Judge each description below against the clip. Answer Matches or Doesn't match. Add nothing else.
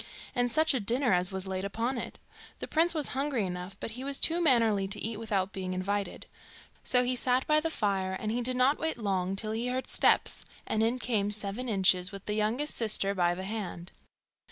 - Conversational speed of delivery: Doesn't match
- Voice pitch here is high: Matches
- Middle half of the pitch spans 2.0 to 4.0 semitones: Doesn't match